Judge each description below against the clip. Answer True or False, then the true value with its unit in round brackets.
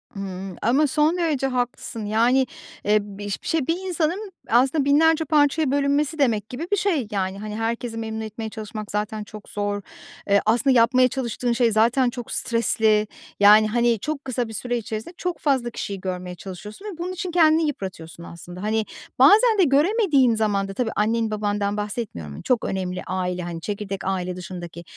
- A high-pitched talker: True (225 Hz)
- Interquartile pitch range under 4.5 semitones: False (5.4 semitones)